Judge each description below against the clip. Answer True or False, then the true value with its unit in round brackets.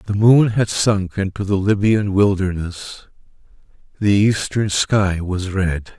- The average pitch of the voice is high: False (100 Hz)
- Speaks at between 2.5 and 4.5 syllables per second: True (3.7 syllables/s)